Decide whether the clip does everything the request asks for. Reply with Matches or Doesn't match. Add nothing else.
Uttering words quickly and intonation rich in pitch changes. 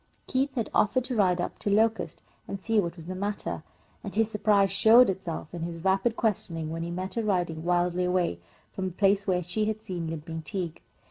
Doesn't match